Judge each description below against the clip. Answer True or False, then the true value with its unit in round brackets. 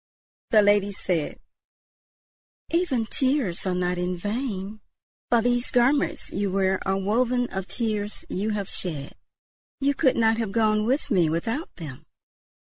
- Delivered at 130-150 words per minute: True (145 wpm)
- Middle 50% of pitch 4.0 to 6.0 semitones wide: True (4.3 semitones)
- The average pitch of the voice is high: True (210 Hz)